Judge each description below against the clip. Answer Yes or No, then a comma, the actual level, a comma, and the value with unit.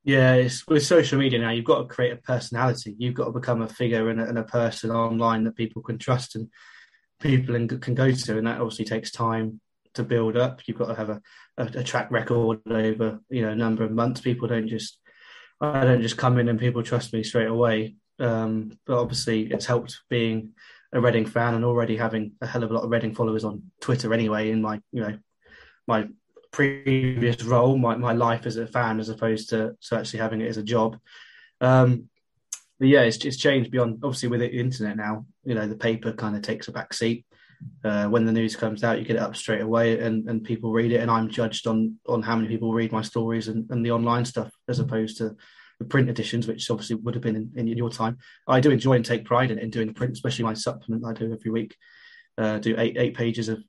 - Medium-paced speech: No, fast, 235 wpm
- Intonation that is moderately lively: No, narrow, 1.6 semitones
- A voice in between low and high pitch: No, low, 115 Hz